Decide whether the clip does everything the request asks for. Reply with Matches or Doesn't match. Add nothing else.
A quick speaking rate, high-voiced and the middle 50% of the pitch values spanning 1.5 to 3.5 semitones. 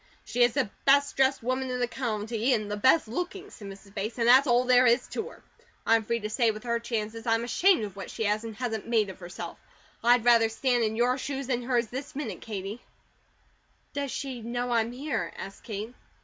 Matches